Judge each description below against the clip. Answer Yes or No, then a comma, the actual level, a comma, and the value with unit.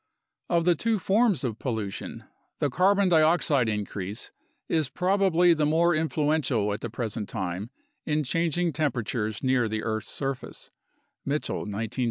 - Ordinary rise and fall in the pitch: No, wide, 7.4 semitones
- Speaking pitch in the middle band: Yes, medium, 145 Hz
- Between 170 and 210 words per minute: No, average, 140 wpm